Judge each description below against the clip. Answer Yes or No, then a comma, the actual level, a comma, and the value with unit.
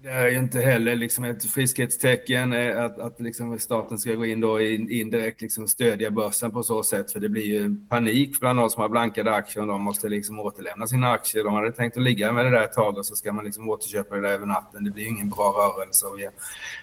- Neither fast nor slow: No, fast, 230 wpm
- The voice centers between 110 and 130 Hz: Yes, low, 115 Hz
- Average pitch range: No, narrow, 2.3 semitones